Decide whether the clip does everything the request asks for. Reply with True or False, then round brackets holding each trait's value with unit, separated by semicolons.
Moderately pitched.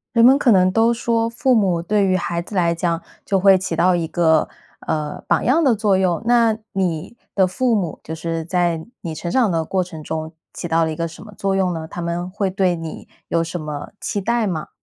True (180 Hz)